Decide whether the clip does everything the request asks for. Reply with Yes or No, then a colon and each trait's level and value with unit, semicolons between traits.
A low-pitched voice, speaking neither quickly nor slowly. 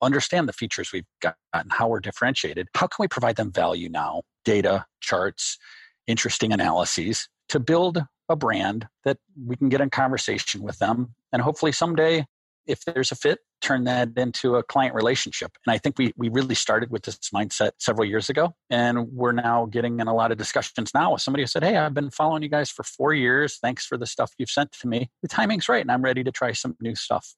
No: low, 130 Hz; fast, 220 wpm